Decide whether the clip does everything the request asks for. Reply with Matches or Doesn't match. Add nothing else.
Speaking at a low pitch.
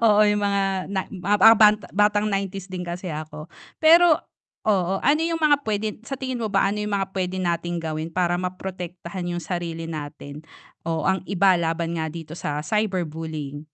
Doesn't match